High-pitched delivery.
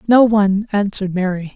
Yes: high, 200 Hz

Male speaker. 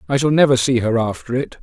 Yes: male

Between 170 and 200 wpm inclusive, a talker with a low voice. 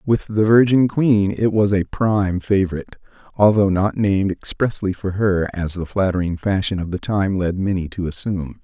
Yes: average, 180 wpm; low, 100 Hz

